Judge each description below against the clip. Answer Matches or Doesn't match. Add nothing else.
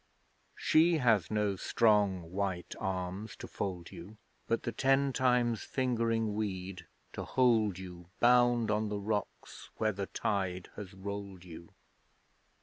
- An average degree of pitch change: Matches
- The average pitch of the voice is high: Doesn't match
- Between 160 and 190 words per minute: Doesn't match